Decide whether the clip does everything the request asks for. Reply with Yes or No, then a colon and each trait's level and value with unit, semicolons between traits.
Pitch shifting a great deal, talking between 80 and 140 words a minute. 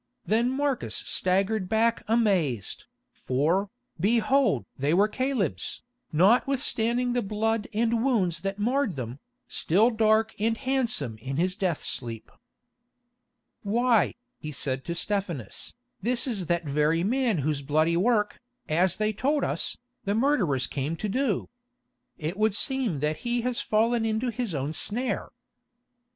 Yes: wide, 6.5 semitones; slow, 135 wpm